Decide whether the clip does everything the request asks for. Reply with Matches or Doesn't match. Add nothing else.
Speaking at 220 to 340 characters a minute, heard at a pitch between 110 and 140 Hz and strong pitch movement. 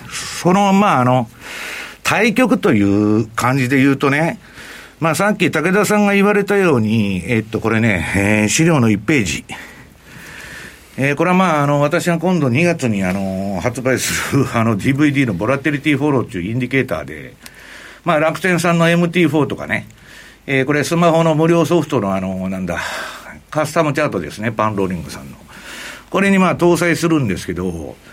Matches